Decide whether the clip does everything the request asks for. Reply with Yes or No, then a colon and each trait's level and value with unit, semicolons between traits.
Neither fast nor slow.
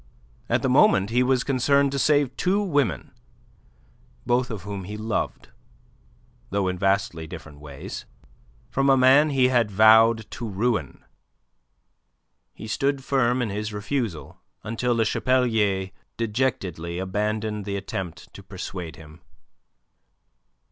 No: slow, 125 wpm